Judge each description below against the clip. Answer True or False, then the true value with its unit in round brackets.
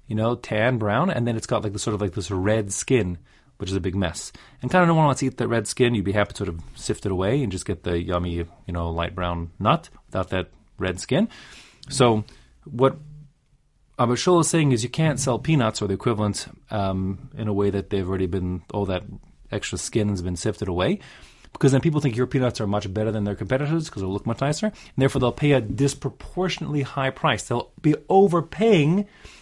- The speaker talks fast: True (230 wpm)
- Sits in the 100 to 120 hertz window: True (110 Hz)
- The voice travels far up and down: True (5.8 semitones)